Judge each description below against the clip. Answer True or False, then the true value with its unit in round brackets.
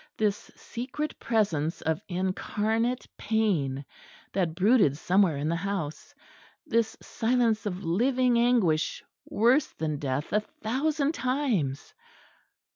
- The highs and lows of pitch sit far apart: True (6.7 semitones)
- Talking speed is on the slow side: True (110 wpm)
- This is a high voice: True (210 Hz)